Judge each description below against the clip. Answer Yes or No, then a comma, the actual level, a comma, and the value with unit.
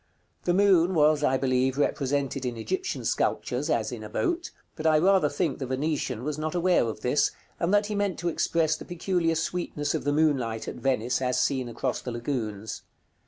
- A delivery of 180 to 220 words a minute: Yes, average, 195 wpm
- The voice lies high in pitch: No, medium, 150 Hz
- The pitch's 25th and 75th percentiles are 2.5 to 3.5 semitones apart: No, average, 5.2 semitones